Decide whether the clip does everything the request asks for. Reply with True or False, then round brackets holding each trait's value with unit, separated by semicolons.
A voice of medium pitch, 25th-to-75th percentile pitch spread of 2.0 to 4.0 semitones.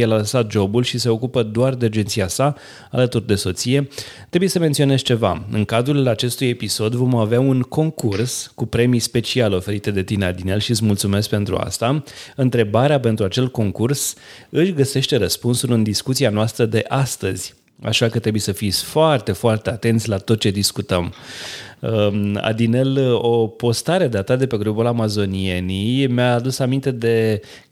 False (115 Hz; 3.4 semitones)